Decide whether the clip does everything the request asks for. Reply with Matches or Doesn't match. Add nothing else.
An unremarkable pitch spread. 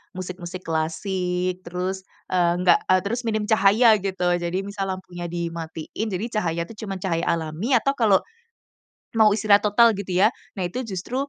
Matches